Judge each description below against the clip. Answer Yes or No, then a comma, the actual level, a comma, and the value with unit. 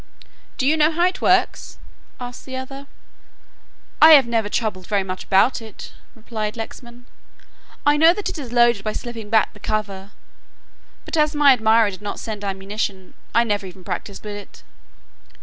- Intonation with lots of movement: No, average, 4.3 semitones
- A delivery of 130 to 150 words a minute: No, average, 170 wpm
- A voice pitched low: No, high, 225 Hz